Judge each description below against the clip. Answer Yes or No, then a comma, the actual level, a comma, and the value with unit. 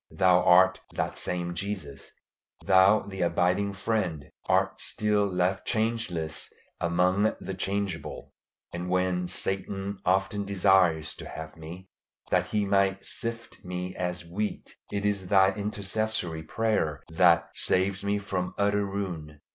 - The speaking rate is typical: No, slow, 130 wpm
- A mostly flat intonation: Yes, narrow, 2.3 semitones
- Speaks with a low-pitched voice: Yes, very low, 95 Hz